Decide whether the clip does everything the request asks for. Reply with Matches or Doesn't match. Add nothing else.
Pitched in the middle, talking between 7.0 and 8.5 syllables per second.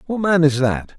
Doesn't match